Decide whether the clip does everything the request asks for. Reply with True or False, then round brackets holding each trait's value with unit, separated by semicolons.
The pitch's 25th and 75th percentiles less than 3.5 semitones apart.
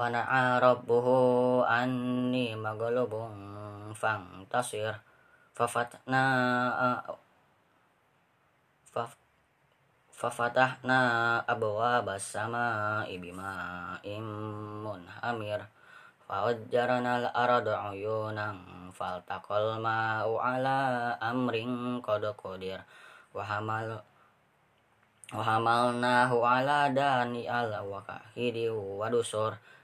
True (2.7 semitones)